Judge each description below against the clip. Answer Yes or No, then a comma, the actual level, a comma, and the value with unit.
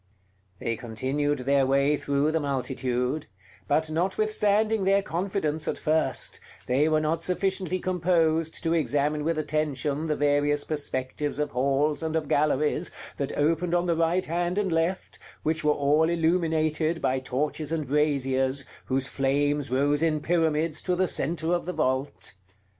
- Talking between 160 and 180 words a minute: No, average, 150 wpm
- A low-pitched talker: No, medium, 155 Hz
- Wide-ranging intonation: No, average, 2.8 semitones